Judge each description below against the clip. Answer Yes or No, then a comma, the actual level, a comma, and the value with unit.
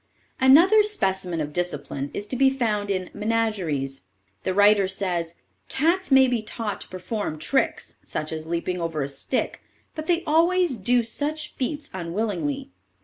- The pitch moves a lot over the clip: Yes, wide, 7.5 semitones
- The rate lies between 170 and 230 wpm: No, average, 155 wpm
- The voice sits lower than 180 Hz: No, high, 210 Hz